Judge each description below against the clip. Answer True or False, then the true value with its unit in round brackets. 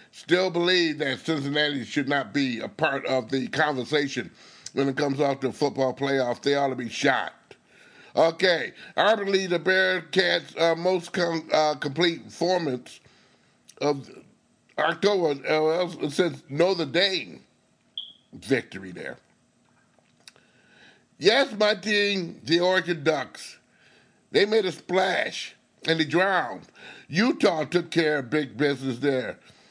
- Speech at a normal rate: False (130 wpm)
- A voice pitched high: False (155 Hz)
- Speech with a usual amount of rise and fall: True (4.3 semitones)